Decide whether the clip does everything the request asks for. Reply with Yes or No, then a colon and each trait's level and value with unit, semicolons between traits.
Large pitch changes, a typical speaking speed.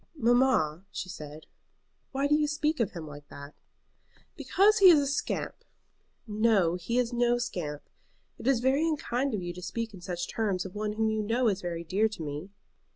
Yes: wide, 6.5 semitones; average, 195 wpm